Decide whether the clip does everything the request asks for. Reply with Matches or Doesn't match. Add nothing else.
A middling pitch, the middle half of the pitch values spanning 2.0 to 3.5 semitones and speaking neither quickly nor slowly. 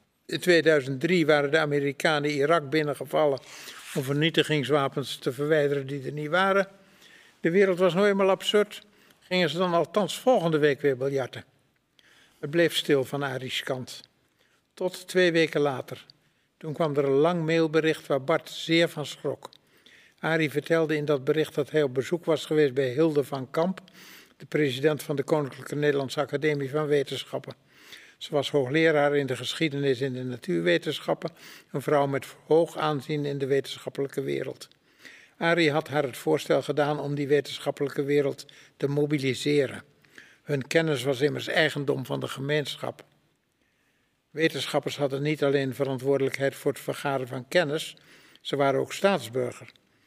Matches